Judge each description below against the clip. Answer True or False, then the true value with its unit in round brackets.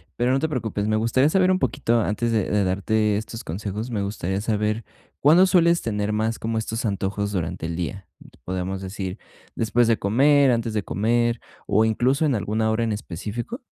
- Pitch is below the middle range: True (110 Hz)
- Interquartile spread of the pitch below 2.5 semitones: False (2.8 semitones)